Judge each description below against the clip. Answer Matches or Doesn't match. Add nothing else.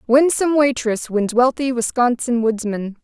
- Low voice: Doesn't match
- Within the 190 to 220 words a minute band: Doesn't match